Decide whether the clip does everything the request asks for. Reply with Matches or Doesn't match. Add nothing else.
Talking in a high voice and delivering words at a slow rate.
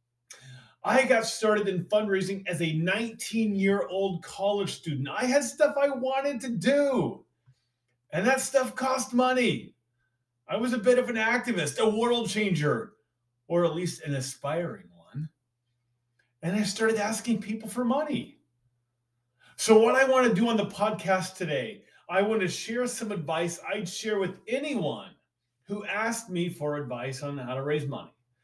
Doesn't match